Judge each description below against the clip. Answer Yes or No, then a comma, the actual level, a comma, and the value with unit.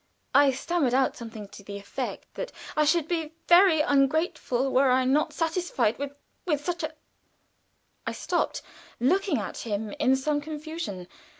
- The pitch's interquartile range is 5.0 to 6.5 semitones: No, average, 4.2 semitones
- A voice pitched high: Yes, very high, 285 Hz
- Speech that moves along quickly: No, average, 160 wpm